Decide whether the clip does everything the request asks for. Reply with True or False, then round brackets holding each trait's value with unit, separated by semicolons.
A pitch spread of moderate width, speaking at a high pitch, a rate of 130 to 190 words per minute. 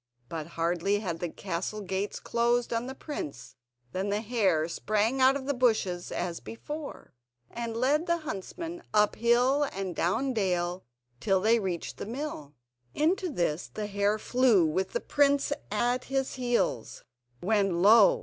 False (5.9 semitones; 215 Hz; 155 wpm)